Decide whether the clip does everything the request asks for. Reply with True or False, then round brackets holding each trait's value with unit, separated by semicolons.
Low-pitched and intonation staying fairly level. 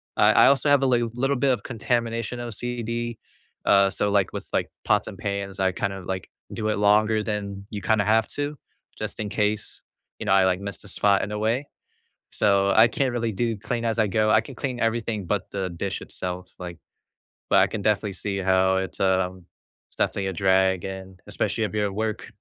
False (105 Hz; 3.1 semitones)